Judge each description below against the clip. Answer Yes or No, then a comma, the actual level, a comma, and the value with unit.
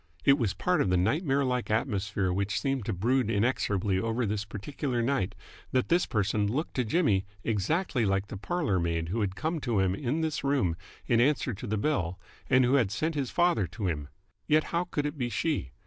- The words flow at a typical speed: No, fast, 210 wpm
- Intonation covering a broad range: Yes, wide, 6.1 semitones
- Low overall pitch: Yes, low, 115 Hz